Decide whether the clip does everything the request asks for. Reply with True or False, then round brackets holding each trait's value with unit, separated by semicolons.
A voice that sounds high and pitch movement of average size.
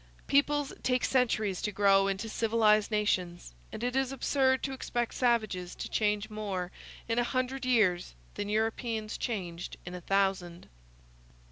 True (215 Hz; 4.1 semitones)